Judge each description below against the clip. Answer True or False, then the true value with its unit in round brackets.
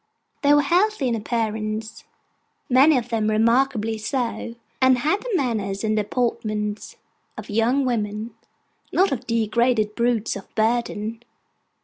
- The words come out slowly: True (125 wpm)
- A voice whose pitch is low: False (230 Hz)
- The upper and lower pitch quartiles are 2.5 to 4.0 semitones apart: True (2.9 semitones)